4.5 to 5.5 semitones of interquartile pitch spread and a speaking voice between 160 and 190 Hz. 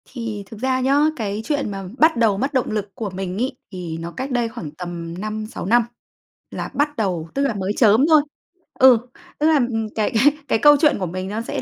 No: average, 5.2 semitones; high, 220 Hz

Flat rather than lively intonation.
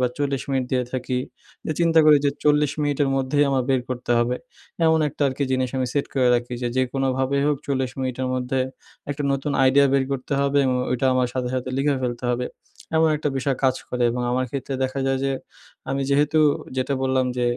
Yes: narrow, 1.7 semitones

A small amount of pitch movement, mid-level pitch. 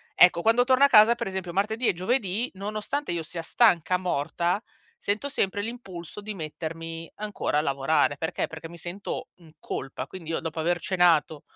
No: average, 4.5 semitones; medium, 180 Hz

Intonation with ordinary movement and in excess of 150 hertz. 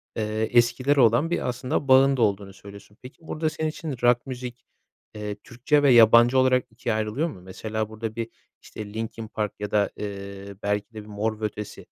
No: average, 3.4 semitones; low, 115 Hz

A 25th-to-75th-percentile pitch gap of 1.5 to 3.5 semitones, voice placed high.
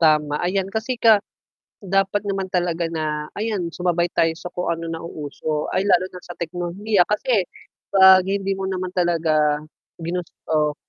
No: average, 2.9 semitones; medium, 180 Hz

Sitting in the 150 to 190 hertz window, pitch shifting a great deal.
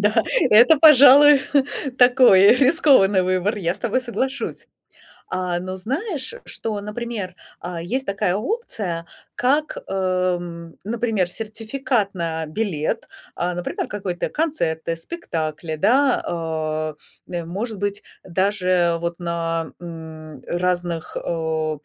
Yes: medium, 185 Hz; wide, 5.9 semitones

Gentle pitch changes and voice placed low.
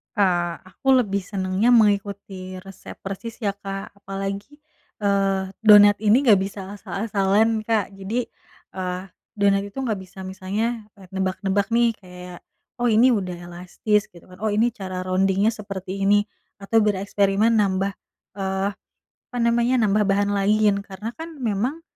No: narrow, 2.1 semitones; high, 200 Hz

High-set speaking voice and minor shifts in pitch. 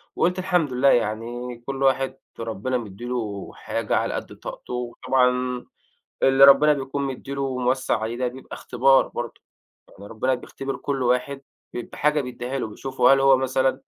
No: low, 130 Hz; narrow, 1.9 semitones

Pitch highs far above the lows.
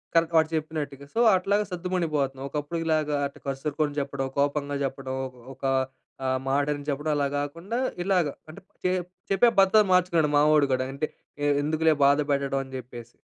No: average, 3.0 semitones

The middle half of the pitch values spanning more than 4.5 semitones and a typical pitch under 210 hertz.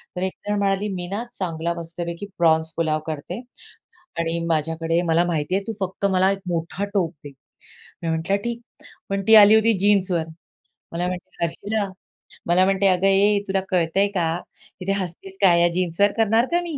No: average, 3.0 semitones; medium, 185 Hz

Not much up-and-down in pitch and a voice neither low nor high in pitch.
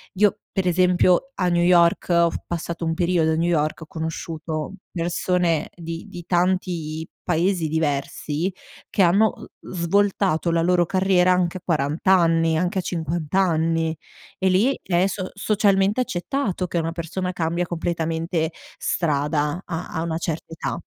Yes: narrow, 2.1 semitones; medium, 170 Hz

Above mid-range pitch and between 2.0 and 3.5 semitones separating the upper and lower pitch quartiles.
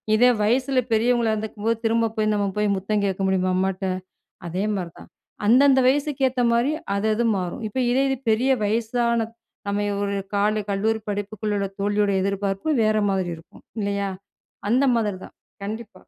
Yes: high, 215 Hz; average, 2.8 semitones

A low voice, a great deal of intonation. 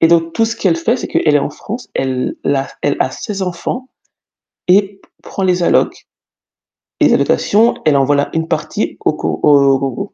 No: medium, 165 Hz; wide, 5.9 semitones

